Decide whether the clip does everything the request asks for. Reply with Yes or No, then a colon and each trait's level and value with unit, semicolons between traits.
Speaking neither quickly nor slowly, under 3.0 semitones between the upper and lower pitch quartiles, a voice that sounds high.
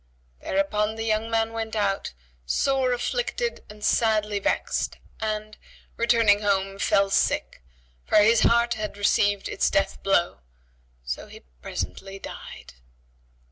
No: slow, 125 wpm; narrow, 2.4 semitones; high, 210 Hz